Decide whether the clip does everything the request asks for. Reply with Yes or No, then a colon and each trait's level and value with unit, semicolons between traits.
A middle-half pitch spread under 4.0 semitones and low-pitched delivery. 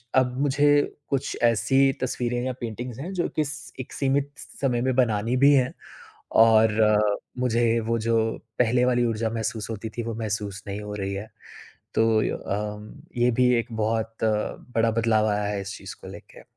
Yes: average, 2.8 semitones; low, 115 Hz